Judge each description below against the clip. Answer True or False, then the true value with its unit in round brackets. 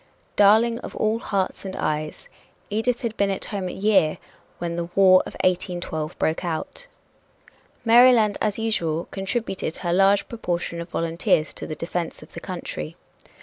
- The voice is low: False (190 Hz)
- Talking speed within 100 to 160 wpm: True (155 wpm)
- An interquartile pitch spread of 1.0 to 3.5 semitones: False (4.3 semitones)